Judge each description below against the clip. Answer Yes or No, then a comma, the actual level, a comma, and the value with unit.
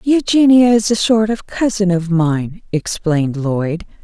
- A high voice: Yes, high, 195 Hz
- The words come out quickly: No, average, 150 wpm